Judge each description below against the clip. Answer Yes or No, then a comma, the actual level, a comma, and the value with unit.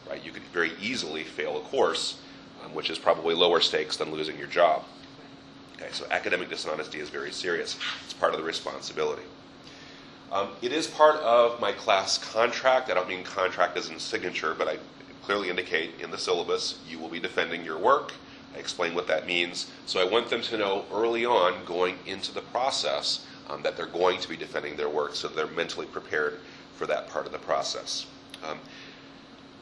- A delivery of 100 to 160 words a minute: No, average, 190 wpm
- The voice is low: No, medium, 155 Hz